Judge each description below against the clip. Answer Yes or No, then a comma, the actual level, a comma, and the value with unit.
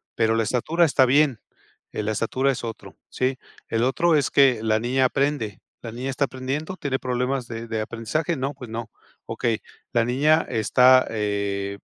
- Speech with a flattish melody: No, average, 3.4 semitones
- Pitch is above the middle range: No, low, 125 Hz